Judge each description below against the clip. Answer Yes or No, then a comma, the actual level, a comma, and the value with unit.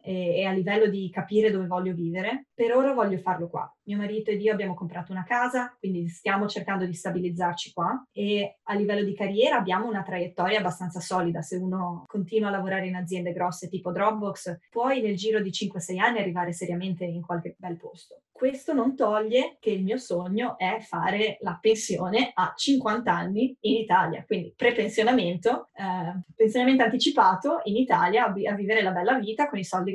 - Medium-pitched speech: No, high, 205 Hz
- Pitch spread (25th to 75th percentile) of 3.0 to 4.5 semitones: Yes, average, 3.6 semitones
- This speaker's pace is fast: Yes, fast, 180 wpm